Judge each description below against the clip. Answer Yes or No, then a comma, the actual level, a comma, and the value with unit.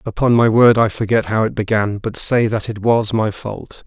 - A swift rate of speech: Yes, fast, 235 wpm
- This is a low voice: Yes, low, 110 Hz